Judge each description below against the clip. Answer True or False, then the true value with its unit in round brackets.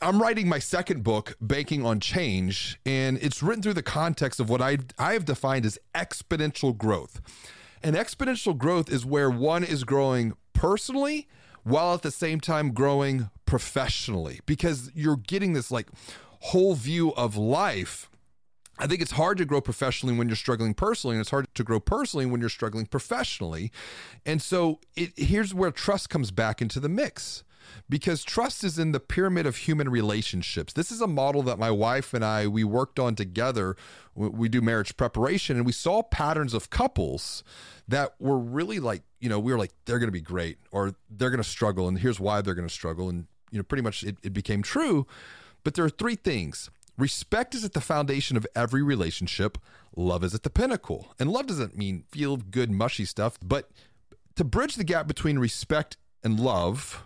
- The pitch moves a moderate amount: False (6.1 semitones)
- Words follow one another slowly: False (190 wpm)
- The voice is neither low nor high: False (130 Hz)